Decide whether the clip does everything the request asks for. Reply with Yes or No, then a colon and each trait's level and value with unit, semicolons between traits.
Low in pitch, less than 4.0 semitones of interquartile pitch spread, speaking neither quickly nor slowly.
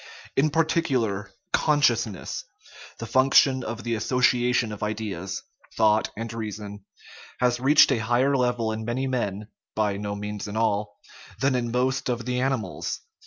Yes: low, 115 Hz; average, 3.3 semitones; average, 145 wpm